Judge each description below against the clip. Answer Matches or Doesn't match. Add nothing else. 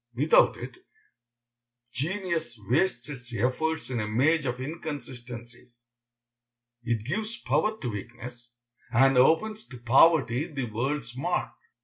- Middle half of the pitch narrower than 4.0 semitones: Doesn't match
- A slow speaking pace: Matches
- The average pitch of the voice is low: Matches